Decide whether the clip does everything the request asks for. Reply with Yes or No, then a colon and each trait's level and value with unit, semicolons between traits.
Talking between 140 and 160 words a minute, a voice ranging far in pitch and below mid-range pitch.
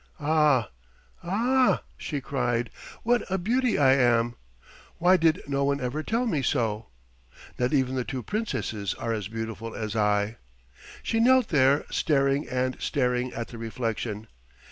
Yes: average, 145 wpm; wide, 5.7 semitones; low, 130 Hz